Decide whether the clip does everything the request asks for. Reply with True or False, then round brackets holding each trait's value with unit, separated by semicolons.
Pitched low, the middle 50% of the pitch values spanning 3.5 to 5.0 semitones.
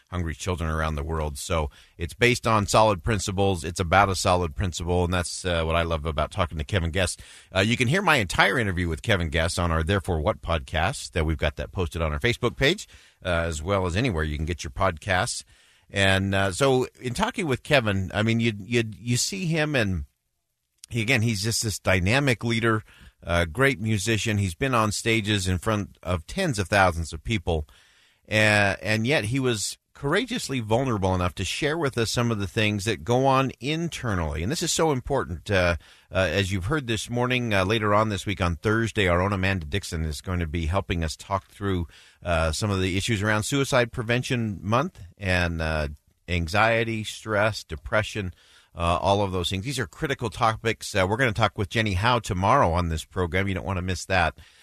True (100 Hz; 4.6 semitones)